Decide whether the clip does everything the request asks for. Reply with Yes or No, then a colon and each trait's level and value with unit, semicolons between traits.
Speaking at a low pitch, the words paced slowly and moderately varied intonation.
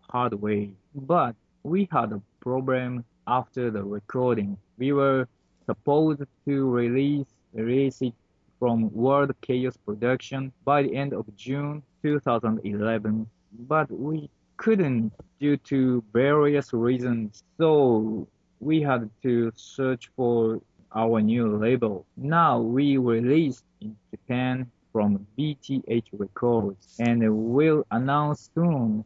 Yes: low, 125 Hz; slow, 115 wpm; average, 4.0 semitones